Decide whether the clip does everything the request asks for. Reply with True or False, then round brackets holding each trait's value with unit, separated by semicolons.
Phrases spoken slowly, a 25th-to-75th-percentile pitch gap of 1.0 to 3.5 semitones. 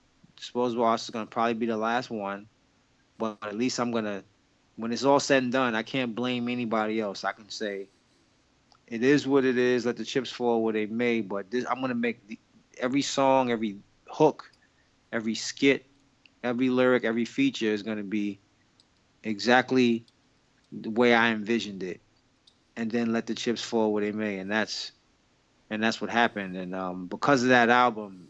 False (180 wpm; 2.8 semitones)